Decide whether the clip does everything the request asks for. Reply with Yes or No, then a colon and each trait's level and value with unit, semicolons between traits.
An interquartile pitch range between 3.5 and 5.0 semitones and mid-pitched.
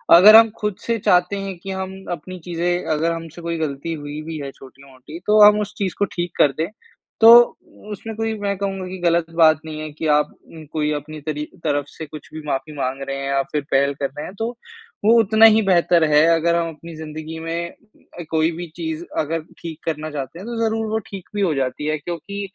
Yes: average, 3.9 semitones; medium, 165 Hz